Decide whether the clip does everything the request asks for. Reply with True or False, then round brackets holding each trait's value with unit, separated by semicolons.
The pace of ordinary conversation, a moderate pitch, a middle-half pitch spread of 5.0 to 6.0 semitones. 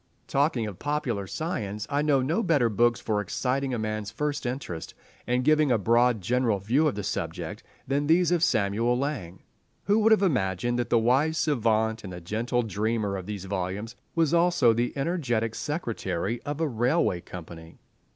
False (170 wpm; 120 Hz; 5.6 semitones)